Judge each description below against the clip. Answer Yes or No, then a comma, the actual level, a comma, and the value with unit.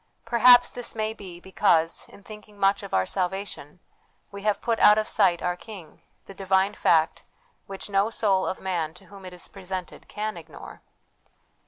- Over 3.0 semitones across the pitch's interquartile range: No, average, 2.7 semitones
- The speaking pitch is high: Yes, high, 195 Hz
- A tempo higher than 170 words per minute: Yes, average, 180 wpm